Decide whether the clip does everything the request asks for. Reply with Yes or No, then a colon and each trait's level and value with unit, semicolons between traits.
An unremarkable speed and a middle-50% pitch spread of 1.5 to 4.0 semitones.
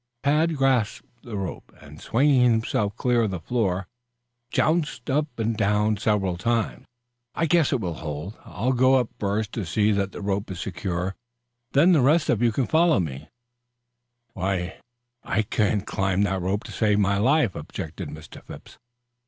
No: average, 170 wpm; average, 4.7 semitones